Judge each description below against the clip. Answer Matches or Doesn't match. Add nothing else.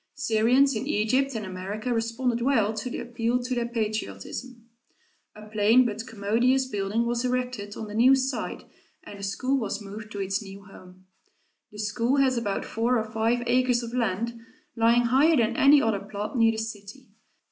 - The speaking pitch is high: Matches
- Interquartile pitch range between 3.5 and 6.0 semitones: Doesn't match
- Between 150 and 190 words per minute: Matches